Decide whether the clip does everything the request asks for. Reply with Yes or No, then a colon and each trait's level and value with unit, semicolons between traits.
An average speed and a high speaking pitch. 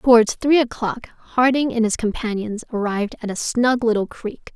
Yes: average, 170 wpm; high, 230 Hz